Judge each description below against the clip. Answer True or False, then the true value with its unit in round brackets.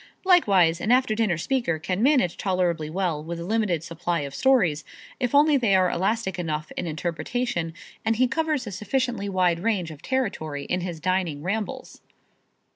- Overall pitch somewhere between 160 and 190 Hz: True (185 Hz)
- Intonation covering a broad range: True (5.7 semitones)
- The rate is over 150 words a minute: True (170 wpm)